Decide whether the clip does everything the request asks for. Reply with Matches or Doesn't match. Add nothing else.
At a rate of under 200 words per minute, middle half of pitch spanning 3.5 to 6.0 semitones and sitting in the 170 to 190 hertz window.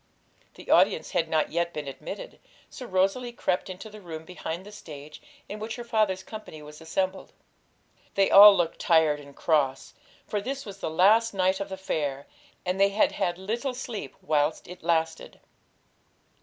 Matches